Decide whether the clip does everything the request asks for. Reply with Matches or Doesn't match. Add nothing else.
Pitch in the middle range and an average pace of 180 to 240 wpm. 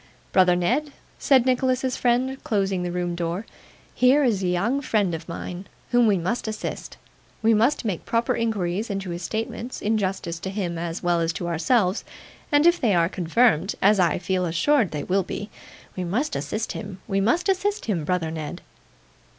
Doesn't match